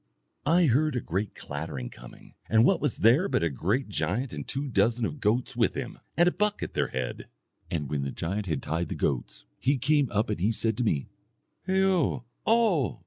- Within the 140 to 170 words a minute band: No, fast, 205 wpm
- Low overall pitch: Yes, low, 115 Hz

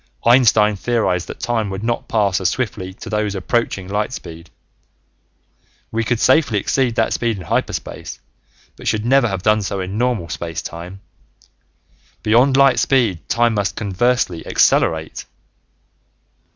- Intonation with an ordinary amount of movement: Yes, average, 4.1 semitones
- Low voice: Yes, low, 105 Hz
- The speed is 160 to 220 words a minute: No, average, 140 wpm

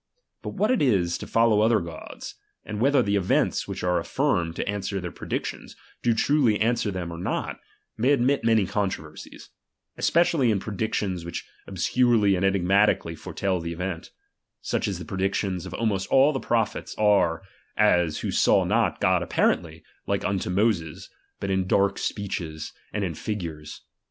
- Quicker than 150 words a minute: Yes, average, 165 wpm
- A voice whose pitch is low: Yes, low, 100 Hz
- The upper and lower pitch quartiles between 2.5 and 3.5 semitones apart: No, average, 4.2 semitones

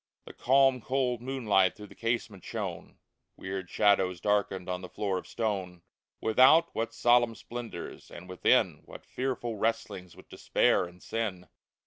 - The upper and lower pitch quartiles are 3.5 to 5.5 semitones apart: Yes, average, 4.6 semitones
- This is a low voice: Yes, low, 105 Hz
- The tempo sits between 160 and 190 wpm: No, average, 145 wpm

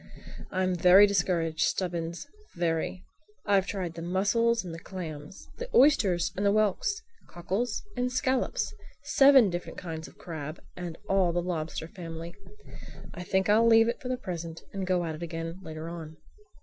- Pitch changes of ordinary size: Yes, average, 3.7 semitones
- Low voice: No, medium, 180 Hz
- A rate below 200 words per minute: Yes, average, 160 wpm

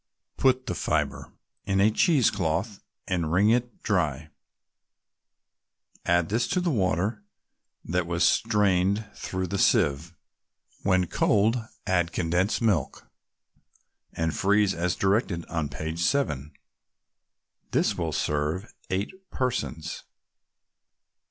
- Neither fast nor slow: No, slow, 110 wpm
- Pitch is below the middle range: Yes, very low, 95 Hz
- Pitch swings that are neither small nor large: Yes, average, 4.5 semitones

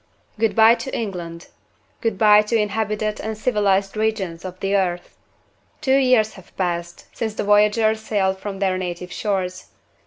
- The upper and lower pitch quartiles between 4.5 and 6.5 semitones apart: No, average, 2.8 semitones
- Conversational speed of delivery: Yes, average, 155 wpm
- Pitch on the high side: Yes, high, 205 Hz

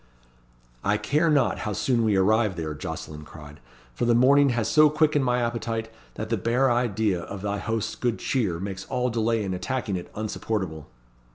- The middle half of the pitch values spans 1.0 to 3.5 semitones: No, average, 4.2 semitones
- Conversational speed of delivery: Yes, average, 180 wpm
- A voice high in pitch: No, low, 110 Hz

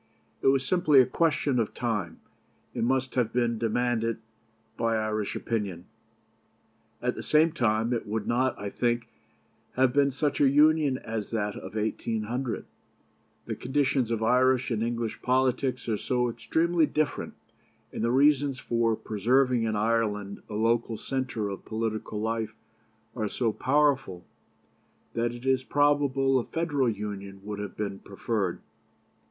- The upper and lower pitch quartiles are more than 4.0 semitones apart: No, average, 3.3 semitones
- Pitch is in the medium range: No, low, 120 Hz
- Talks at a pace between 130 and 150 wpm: Yes, average, 145 wpm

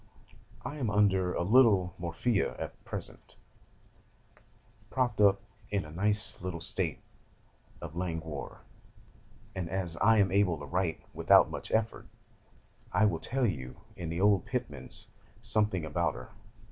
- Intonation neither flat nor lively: Yes, average, 3.8 semitones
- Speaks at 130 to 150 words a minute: Yes, slow, 135 wpm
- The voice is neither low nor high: No, very low, 95 Hz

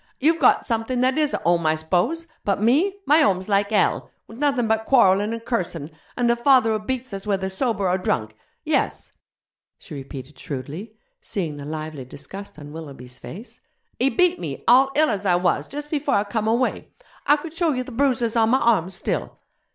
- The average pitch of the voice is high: Yes, high, 220 Hz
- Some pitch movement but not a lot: No, wide, 6.6 semitones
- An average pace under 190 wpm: No, average, 195 wpm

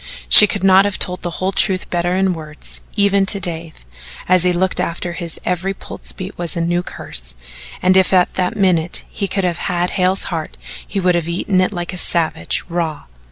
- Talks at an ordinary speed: No, fast, 215 wpm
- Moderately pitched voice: Yes, medium, 180 Hz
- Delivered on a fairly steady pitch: Yes, narrow, 1.8 semitones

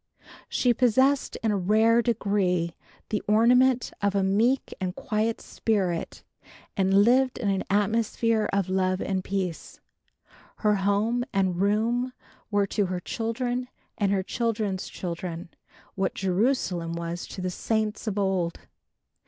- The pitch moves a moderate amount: Yes, average, 3.4 semitones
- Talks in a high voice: Yes, high, 205 Hz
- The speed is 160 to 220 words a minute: No, slow, 135 wpm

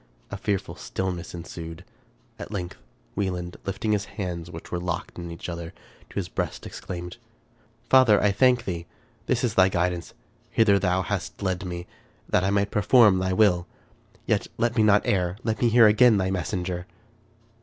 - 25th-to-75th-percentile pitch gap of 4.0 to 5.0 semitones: No, average, 3.0 semitones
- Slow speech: No, average, 175 wpm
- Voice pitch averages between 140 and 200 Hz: No, very low, 95 Hz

